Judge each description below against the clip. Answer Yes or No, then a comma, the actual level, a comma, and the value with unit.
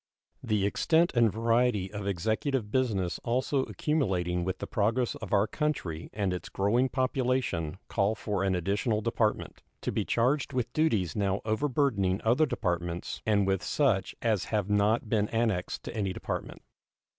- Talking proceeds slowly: No, average, 155 wpm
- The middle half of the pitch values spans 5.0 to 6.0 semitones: No, average, 4.3 semitones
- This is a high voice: No, low, 105 Hz